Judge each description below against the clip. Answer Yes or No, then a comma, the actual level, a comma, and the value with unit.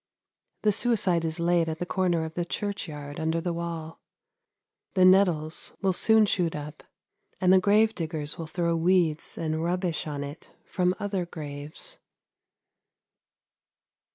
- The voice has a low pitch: No, medium, 170 Hz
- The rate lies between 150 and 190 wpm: No, average, 140 wpm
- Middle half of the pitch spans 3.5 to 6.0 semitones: No, average, 2.7 semitones